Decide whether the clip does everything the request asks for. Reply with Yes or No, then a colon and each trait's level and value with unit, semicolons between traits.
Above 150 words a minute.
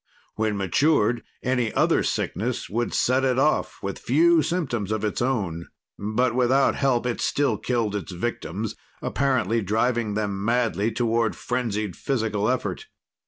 No: average, 140 wpm